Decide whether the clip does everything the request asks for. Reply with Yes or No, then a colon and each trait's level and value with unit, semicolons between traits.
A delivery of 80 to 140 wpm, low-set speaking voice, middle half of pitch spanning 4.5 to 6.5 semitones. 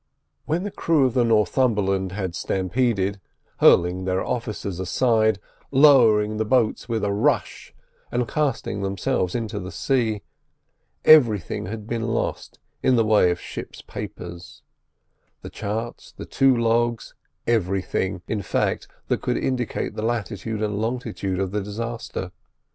No: slow, 135 wpm; low, 110 Hz; average, 3.5 semitones